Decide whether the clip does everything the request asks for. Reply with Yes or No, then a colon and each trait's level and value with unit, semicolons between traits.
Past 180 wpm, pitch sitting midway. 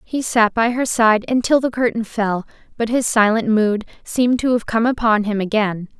No: average, 200 wpm; high, 225 Hz